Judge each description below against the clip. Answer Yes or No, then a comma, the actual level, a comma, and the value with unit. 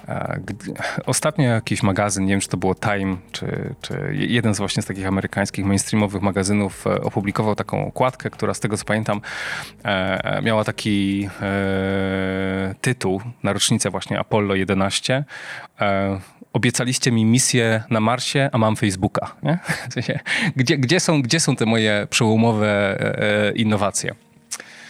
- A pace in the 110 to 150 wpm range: Yes, average, 135 wpm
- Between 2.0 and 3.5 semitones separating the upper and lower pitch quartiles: No, average, 4.0 semitones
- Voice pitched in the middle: No, low, 105 Hz